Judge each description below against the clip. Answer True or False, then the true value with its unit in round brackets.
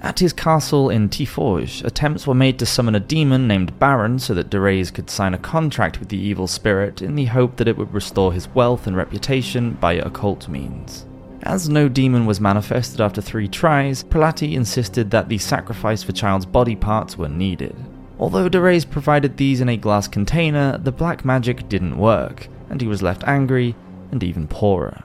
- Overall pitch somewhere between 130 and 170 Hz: False (115 Hz)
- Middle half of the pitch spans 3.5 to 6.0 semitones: True (5.6 semitones)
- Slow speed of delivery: False (190 wpm)